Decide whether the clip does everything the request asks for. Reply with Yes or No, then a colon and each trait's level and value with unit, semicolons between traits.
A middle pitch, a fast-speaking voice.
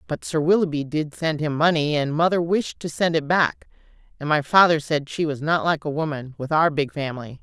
Yes: medium, 155 Hz; fast, 220 wpm